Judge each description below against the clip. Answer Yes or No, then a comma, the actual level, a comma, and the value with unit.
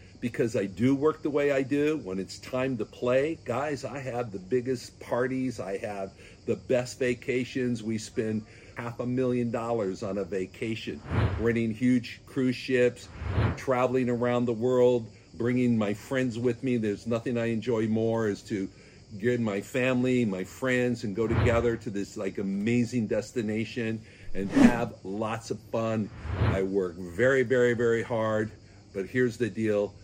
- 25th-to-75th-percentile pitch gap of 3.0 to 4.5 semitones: Yes, average, 3.4 semitones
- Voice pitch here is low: Yes, low, 115 Hz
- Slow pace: No, average, 160 wpm